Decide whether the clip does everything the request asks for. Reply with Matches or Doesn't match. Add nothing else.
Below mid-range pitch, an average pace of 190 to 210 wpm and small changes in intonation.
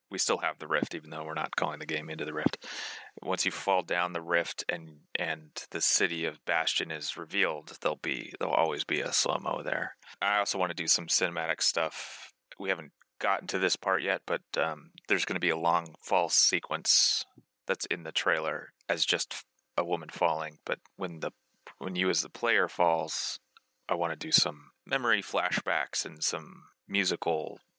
Matches